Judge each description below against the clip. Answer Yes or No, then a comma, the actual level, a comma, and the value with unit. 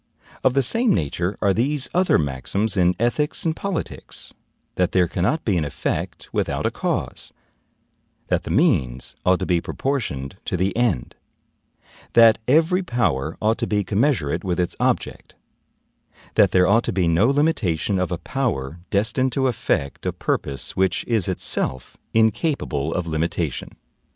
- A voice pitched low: Yes, low, 100 Hz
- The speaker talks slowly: No, average, 155 wpm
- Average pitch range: No, wide, 7.3 semitones